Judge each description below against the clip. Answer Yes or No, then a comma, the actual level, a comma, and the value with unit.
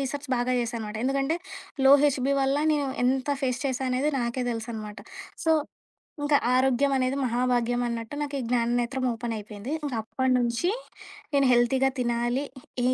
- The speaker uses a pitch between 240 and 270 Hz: Yes, very high, 255 Hz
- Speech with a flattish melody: Yes, narrow, 2.3 semitones